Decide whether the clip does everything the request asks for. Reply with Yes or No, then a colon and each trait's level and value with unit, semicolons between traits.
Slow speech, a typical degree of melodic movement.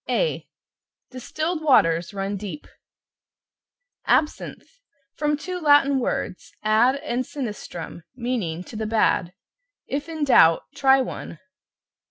No: slow, 110 wpm; wide, 6.3 semitones